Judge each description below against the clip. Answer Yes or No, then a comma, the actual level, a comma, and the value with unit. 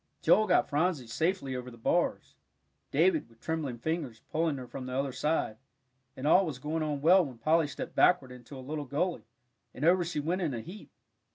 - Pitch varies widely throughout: No, average, 4.5 semitones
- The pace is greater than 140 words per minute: Yes, average, 200 wpm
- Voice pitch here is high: No, medium, 150 Hz